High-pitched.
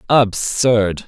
No: low, 110 Hz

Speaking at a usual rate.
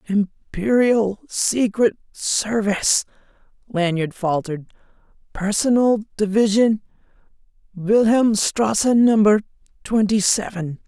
No: slow, 50 wpm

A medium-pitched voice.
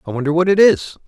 Yes: medium, 155 Hz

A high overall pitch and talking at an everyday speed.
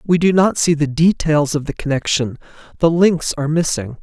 No: medium, 155 Hz; average, 195 wpm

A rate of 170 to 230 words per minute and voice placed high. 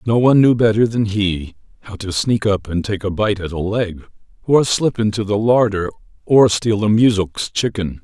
No: average, 200 wpm; low, 105 Hz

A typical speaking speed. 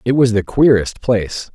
Yes: average, 195 wpm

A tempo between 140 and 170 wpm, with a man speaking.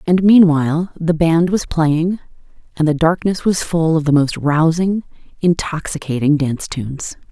No: average, 150 wpm; female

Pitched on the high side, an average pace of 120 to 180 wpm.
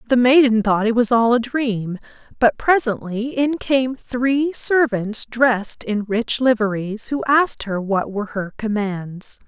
Yes: high, 230 Hz; average, 160 wpm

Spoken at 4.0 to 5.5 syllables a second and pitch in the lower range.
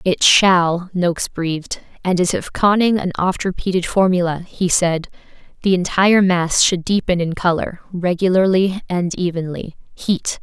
No: 4.5 syllables/s; medium, 180 Hz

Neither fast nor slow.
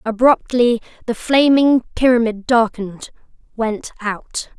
No: slow, 80 wpm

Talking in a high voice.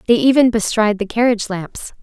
Yes: high, 220 Hz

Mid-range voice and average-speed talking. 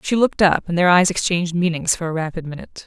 No: medium, 175 Hz; fast, 250 wpm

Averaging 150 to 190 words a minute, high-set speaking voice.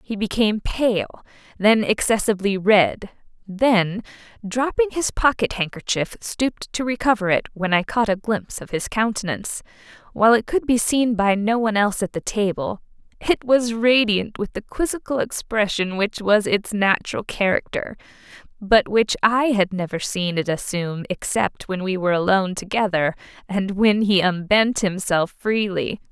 Yes: average, 155 wpm; high, 210 Hz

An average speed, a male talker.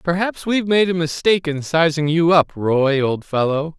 Yes: average, 190 wpm; male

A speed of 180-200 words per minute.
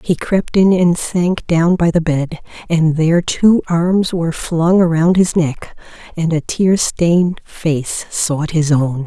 No: average, 170 wpm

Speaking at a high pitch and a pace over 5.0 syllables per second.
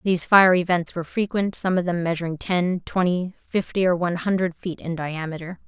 No: medium, 175 Hz; 5.5 syllables/s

